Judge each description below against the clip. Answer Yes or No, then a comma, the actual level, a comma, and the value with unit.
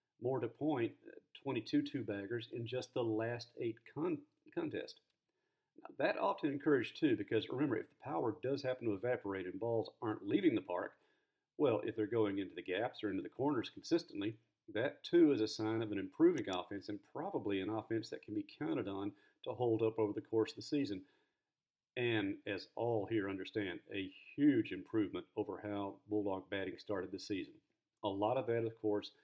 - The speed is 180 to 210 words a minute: Yes, average, 190 wpm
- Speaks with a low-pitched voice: Yes, low, 125 Hz